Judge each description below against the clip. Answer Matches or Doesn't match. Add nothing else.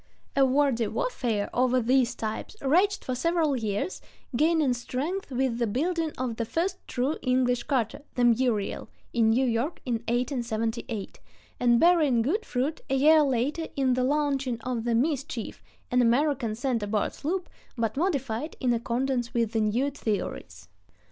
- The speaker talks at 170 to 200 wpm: Doesn't match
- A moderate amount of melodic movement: Matches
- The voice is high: Matches